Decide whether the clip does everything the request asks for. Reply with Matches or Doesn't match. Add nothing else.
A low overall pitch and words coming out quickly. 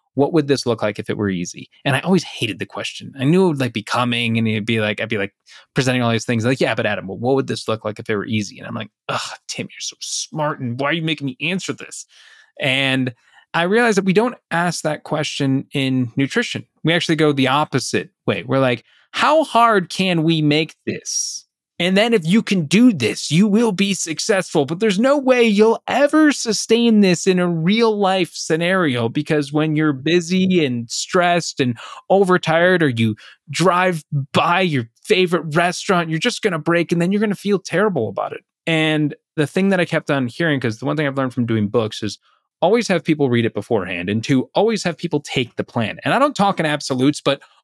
Doesn't match